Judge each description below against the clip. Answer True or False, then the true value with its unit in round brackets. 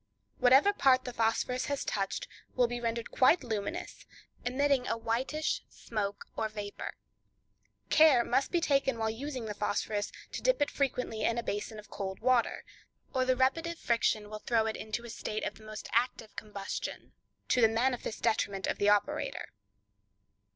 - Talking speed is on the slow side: False (165 wpm)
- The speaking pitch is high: True (235 Hz)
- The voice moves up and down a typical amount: True (3.4 semitones)